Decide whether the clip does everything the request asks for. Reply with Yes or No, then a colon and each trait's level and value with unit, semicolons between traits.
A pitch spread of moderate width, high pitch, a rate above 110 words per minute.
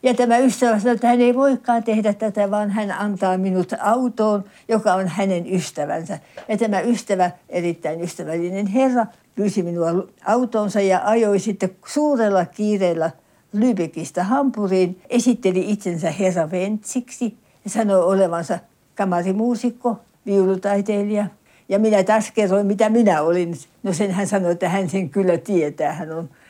Yes: average, 3.3 semitones; high, 200 Hz; average, 140 wpm